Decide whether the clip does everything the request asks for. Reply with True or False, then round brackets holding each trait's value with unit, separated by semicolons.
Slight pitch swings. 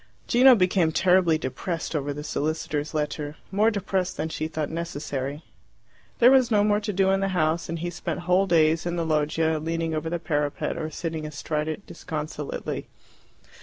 False (3.2 semitones)